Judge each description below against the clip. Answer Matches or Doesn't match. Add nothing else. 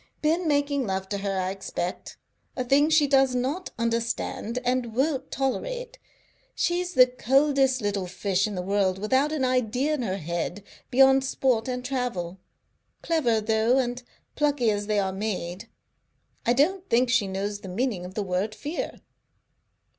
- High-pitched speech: Matches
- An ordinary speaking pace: Matches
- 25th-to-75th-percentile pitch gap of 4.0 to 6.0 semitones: Matches